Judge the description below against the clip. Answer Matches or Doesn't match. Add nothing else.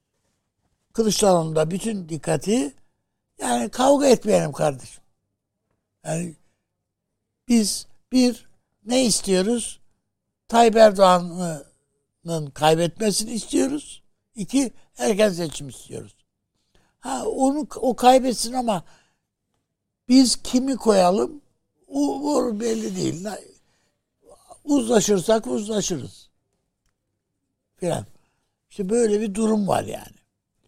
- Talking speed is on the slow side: Matches